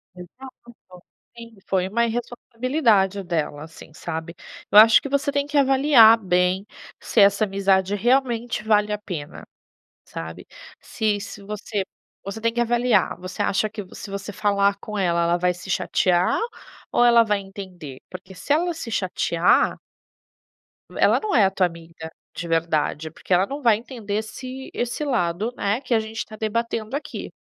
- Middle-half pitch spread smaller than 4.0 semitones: No, average, 4.4 semitones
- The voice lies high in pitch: Yes, high, 210 Hz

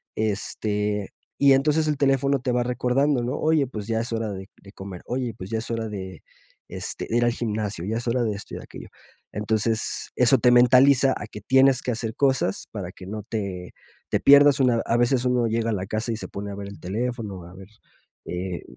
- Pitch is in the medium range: No, low, 115 Hz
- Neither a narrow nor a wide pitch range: Yes, average, 3.5 semitones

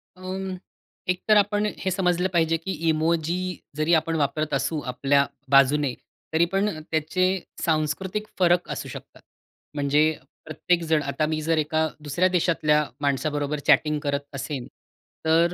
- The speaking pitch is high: No, medium, 160 Hz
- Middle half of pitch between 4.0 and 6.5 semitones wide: No, average, 3.1 semitones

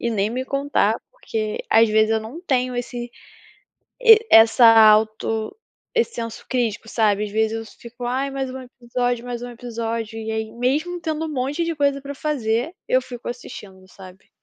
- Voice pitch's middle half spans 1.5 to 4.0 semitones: Yes, average, 3.6 semitones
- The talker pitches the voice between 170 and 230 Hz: No, high, 240 Hz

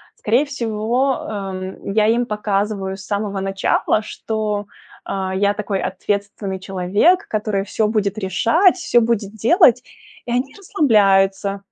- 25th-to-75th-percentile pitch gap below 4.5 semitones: Yes, average, 2.9 semitones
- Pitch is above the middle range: Yes, high, 210 Hz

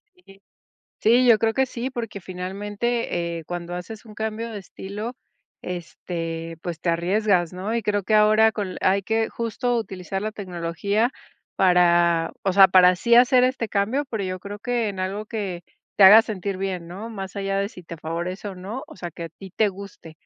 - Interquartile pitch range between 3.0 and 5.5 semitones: Yes, average, 3.5 semitones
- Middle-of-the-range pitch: No, high, 195 Hz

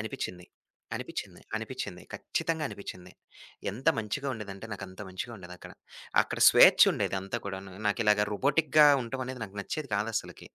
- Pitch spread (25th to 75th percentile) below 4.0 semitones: No, average, 5.0 semitones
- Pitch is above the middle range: No, low, 105 Hz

